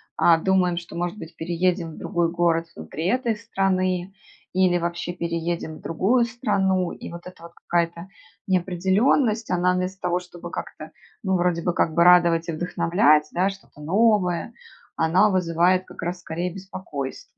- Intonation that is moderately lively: No, narrow, 2.0 semitones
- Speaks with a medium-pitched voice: Yes, medium, 175 Hz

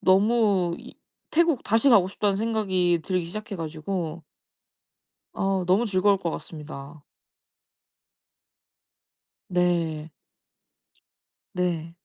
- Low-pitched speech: No, medium, 185 Hz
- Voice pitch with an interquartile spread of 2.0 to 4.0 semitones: Yes, average, 3.5 semitones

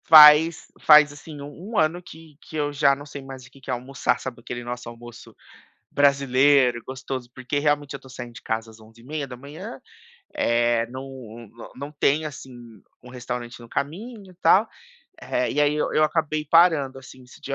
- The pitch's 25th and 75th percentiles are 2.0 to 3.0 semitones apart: No, average, 3.6 semitones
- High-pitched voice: No, medium, 140 Hz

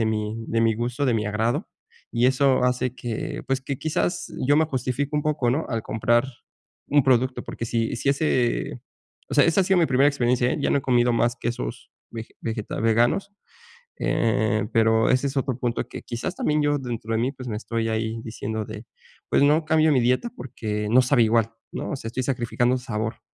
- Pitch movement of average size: Yes, average, 3.3 semitones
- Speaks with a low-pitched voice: Yes, low, 120 Hz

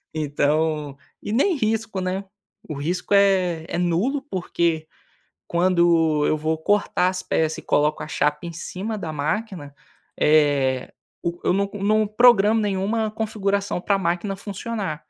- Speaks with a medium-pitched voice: Yes, medium, 180 Hz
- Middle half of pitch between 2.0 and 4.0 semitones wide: No, average, 4.7 semitones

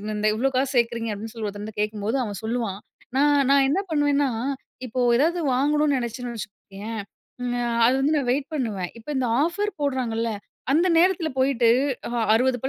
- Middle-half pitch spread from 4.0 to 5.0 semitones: Yes, average, 4.5 semitones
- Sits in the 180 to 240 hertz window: No, very high, 250 Hz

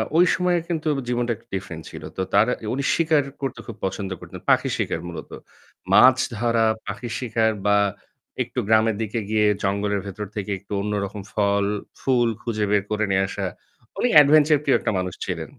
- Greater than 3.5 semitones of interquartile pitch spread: Yes, average, 4.0 semitones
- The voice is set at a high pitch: No, low, 110 Hz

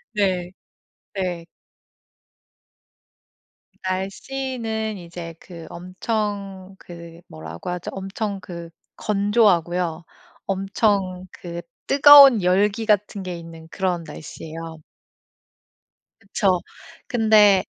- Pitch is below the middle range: No, high, 190 Hz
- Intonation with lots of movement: No, average, 3.2 semitones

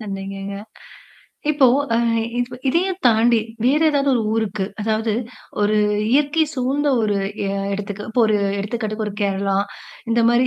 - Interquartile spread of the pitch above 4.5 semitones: No, average, 3.9 semitones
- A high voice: Yes, high, 225 Hz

